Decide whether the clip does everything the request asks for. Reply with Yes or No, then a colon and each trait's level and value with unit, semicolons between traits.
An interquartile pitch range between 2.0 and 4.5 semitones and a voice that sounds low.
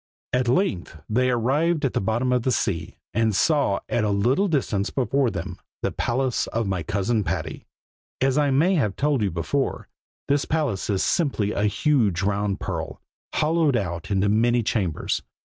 No: wide, 5.6 semitones; low, 115 Hz